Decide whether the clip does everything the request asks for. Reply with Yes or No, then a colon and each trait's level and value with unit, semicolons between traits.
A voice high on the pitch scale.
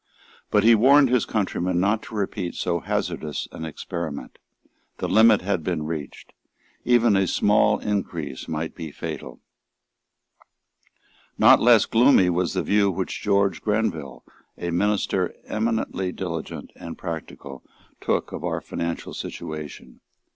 No: very low, 95 Hz